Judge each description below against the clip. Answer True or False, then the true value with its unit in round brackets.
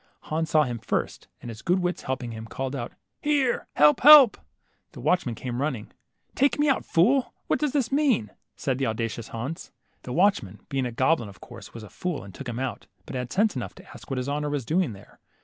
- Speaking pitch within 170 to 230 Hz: False (135 Hz)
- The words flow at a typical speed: False (235 wpm)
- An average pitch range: False (7.8 semitones)